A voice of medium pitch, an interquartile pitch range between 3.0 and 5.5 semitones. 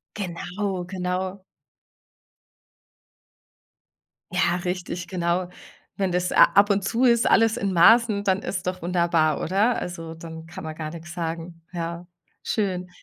No: medium, 180 Hz; narrow, 2.5 semitones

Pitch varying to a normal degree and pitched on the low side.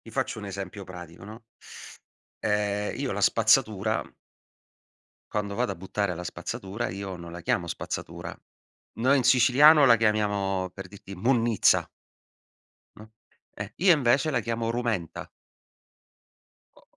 Yes: average, 3.7 semitones; low, 105 Hz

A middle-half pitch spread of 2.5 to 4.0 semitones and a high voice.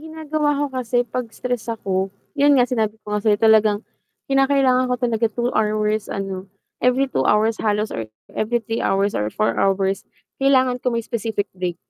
Yes: average, 3.4 semitones; high, 225 Hz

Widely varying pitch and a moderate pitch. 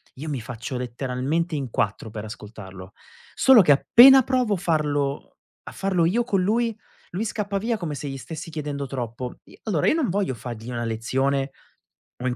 Yes: wide, 7.9 semitones; medium, 145 Hz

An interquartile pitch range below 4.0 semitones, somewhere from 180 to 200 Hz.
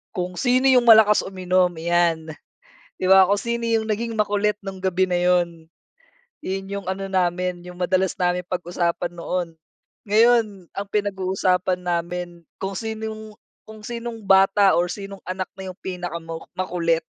Yes: average, 2.8 semitones; high, 190 Hz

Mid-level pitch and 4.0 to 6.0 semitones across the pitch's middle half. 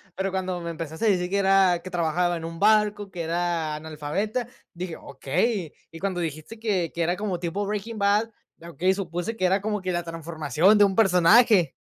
No: medium, 180 Hz; average, 3.3 semitones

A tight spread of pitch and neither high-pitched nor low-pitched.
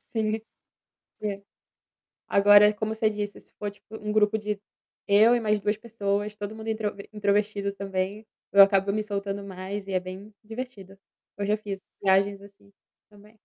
No: narrow, 1.3 semitones; high, 205 Hz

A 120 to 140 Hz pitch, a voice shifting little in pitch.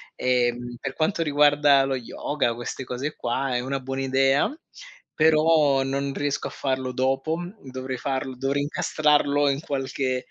Yes: low, 135 Hz; narrow, 1.9 semitones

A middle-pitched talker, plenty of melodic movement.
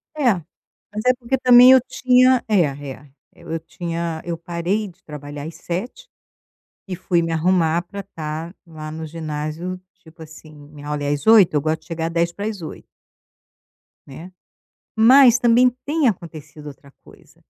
Yes: medium, 170 Hz; wide, 5.7 semitones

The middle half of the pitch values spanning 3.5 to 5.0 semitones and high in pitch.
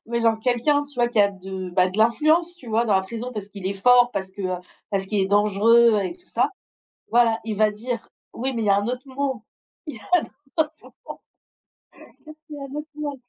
Yes: average, 4.4 semitones; high, 230 Hz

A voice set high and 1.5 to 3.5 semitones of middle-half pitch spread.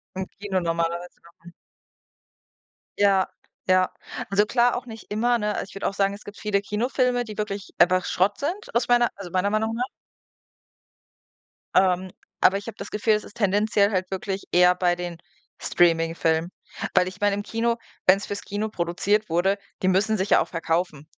Yes: high, 200 Hz; average, 2.8 semitones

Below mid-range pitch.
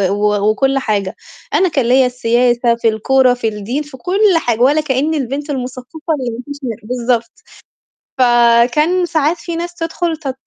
No: very high, 255 Hz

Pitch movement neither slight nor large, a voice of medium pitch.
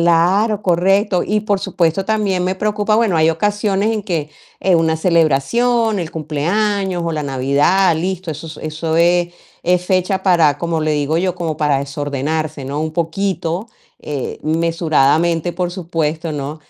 Yes: average, 3.6 semitones; medium, 170 Hz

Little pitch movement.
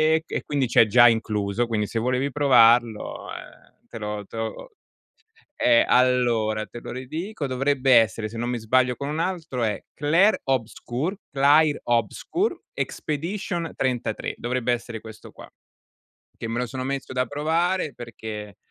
No: average, 4.1 semitones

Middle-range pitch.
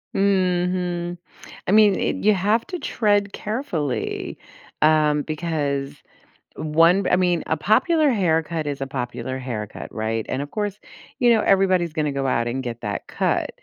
Yes: medium, 170 Hz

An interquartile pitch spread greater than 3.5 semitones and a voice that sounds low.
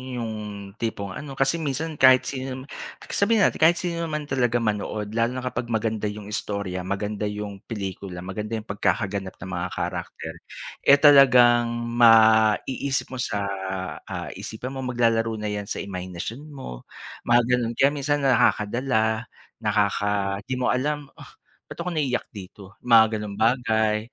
Yes: average, 4.1 semitones; low, 115 Hz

